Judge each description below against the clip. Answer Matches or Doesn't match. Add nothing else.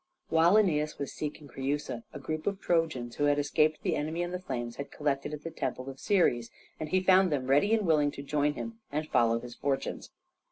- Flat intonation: Doesn't match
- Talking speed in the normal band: Doesn't match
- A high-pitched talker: Doesn't match